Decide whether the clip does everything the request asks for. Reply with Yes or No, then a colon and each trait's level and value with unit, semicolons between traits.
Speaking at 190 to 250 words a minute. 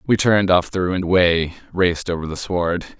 Yes: average, 200 wpm